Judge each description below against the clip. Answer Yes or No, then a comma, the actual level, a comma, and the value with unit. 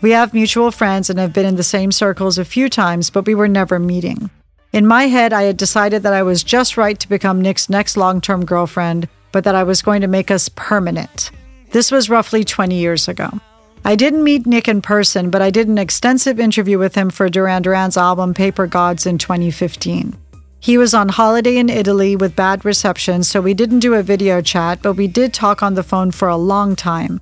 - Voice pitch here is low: No, high, 195 Hz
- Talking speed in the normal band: No, fast, 225 wpm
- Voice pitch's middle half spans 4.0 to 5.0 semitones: No, average, 2.8 semitones